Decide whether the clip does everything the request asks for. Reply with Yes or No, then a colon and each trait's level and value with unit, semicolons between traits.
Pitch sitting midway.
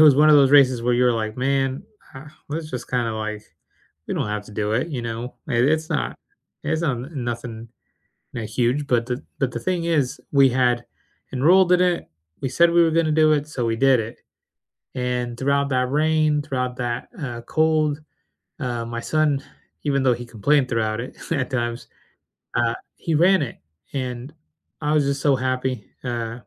No: low, 130 Hz